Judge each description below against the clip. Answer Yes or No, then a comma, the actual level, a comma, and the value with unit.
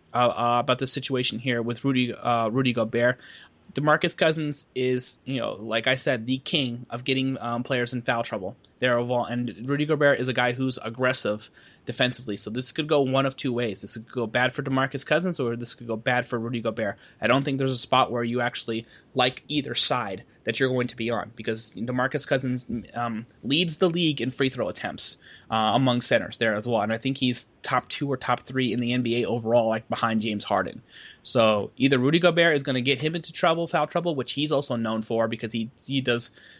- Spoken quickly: Yes, fast, 225 wpm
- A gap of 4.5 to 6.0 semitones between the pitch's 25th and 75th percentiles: No, narrow, 2.5 semitones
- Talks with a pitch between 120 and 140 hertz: Yes, low, 125 Hz